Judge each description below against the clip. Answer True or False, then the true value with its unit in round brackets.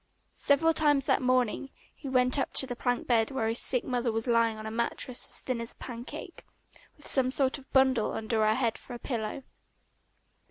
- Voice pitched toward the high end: True (250 Hz)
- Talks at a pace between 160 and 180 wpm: False (205 wpm)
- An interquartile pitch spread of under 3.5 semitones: True (2.6 semitones)